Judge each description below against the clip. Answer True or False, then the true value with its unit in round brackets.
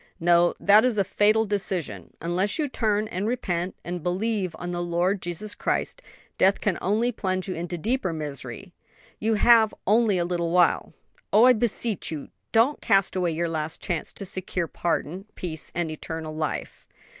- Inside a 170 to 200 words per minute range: True (175 wpm)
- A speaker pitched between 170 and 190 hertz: True (185 Hz)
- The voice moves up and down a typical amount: True (3.7 semitones)